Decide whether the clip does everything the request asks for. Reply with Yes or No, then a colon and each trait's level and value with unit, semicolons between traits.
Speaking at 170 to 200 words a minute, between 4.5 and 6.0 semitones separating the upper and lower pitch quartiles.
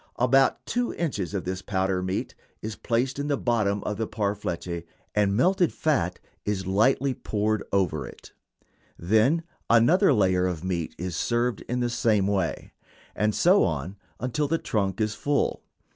No: average, 160 wpm; average, 5.1 semitones